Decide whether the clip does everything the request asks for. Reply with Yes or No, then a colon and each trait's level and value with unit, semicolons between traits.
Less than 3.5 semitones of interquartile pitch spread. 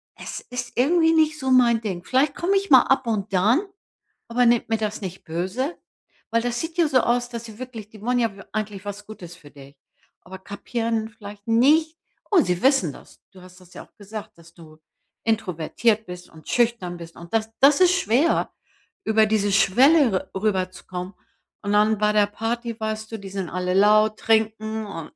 No: average, 4.2 semitones